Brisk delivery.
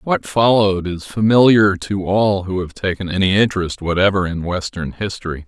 No: average, 165 wpm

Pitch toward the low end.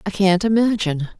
No: high, 195 Hz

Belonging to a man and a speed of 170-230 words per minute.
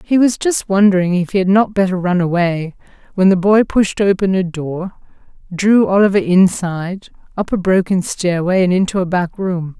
No: female; average, 185 wpm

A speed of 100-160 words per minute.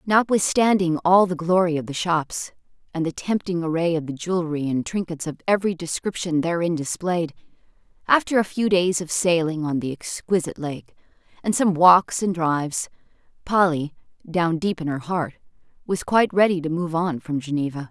No: average, 170 wpm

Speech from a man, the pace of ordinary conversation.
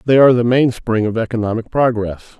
Yes: male; average, 175 wpm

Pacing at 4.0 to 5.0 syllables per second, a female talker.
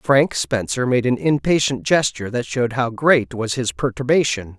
No: 4.8 syllables/s; male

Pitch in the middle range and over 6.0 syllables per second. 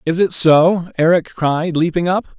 No: medium, 165 Hz; 4.1 syllables/s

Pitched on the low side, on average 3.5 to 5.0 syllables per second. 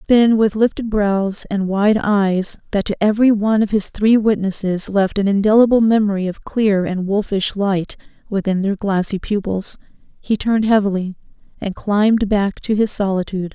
No: high, 205 Hz; 4.9 syllables/s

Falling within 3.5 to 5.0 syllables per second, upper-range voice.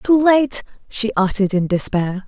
Yes: 4.7 syllables/s; high, 230 Hz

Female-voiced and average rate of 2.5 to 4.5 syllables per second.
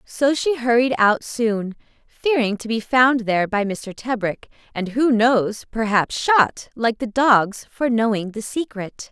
Yes: female; 3.9 syllables/s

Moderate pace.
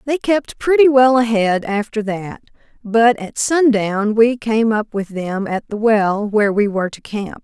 Yes: average, 185 wpm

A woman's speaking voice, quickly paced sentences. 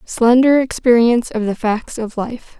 No: female; average, 160 wpm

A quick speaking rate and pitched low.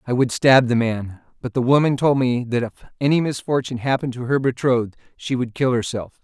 Yes: fast, 210 wpm; low, 125 Hz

